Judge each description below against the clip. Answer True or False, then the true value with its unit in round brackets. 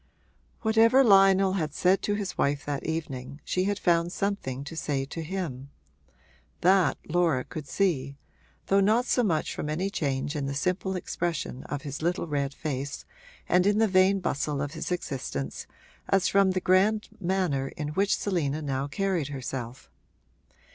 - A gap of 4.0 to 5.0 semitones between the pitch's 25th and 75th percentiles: False (5.5 semitones)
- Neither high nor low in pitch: True (165 Hz)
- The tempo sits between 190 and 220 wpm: False (160 wpm)